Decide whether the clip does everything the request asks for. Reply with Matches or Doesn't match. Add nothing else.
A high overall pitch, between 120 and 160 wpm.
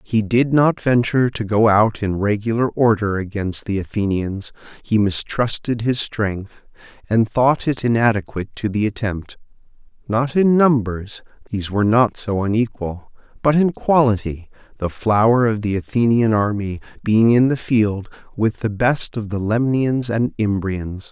Doesn't match